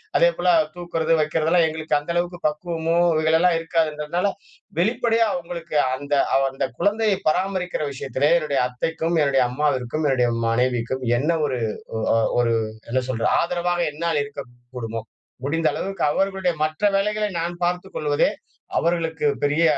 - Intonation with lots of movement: No, average, 3.7 semitones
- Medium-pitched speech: Yes, medium, 160 Hz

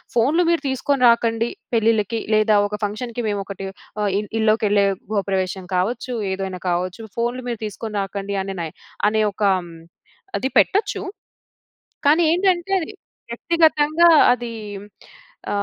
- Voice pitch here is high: Yes, high, 225 Hz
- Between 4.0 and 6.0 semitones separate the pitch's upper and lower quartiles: Yes, average, 4.4 semitones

